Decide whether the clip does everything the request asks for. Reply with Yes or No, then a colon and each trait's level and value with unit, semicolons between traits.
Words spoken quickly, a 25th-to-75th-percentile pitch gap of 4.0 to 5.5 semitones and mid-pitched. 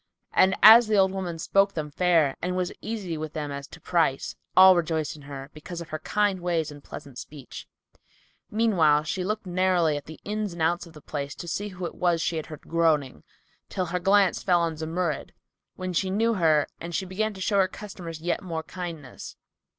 No: fast, 210 wpm; average, 3.2 semitones; medium, 175 Hz